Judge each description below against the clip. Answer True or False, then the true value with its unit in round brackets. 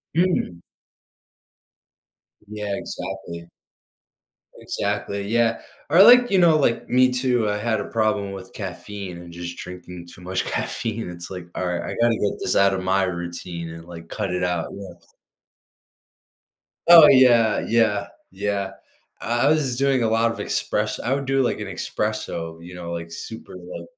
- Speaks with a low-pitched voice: True (100 Hz)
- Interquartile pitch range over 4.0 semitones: True (4.9 semitones)